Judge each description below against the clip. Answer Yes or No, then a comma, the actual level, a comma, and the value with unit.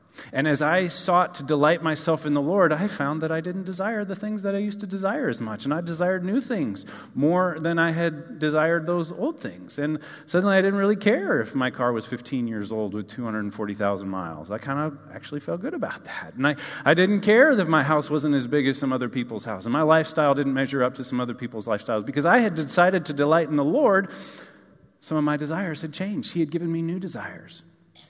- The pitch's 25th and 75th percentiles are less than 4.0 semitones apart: No, average, 5.0 semitones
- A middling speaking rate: No, fast, 235 wpm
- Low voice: No, medium, 155 Hz